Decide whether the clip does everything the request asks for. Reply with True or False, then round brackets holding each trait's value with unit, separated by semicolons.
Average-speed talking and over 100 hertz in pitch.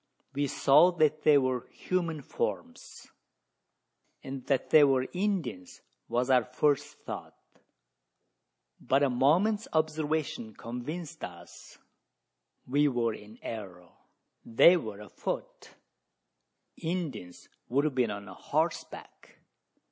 False (105 wpm; 135 Hz)